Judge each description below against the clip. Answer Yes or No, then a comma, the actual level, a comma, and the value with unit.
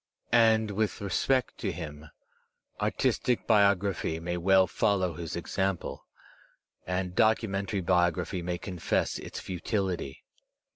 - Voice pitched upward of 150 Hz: No, very low, 95 Hz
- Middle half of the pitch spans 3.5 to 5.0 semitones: No, average, 2.7 semitones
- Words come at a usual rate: No, slow, 110 wpm